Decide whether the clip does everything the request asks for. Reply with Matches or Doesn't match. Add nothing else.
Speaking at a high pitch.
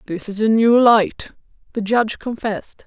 Matches